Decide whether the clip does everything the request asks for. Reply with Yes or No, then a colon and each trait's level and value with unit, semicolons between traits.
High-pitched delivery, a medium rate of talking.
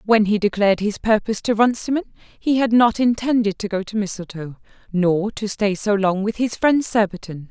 Yes: high, 210 Hz; average, 190 wpm